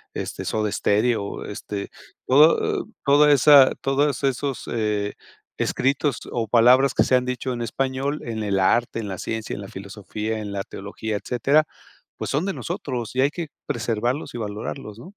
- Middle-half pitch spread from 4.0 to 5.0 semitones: Yes, average, 4.3 semitones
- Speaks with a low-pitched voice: Yes, low, 120 Hz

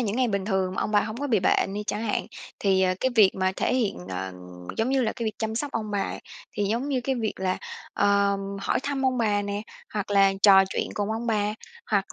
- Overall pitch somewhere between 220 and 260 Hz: No, high, 210 Hz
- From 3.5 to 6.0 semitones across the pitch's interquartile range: No, average, 2.8 semitones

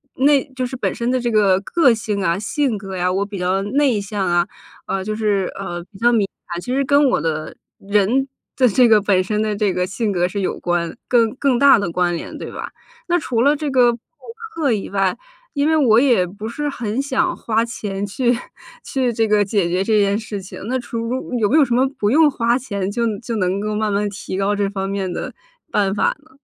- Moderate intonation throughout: Yes, average, 4.3 semitones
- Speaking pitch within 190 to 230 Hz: Yes, high, 210 Hz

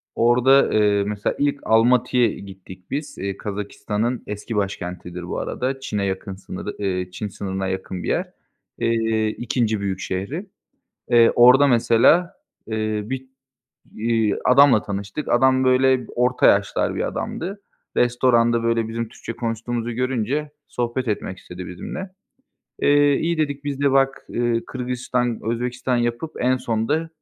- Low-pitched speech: Yes, low, 115 Hz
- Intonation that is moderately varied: Yes, average, 3.8 semitones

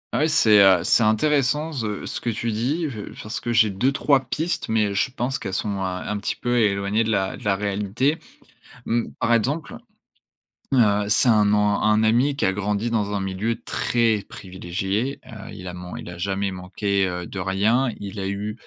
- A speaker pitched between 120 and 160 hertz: No, low, 105 Hz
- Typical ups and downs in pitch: Yes, average, 3.5 semitones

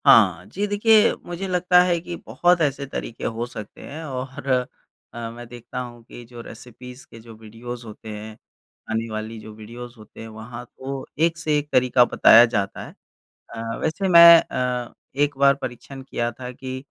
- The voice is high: No, low, 125 Hz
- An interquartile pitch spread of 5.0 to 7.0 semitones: No, average, 4.3 semitones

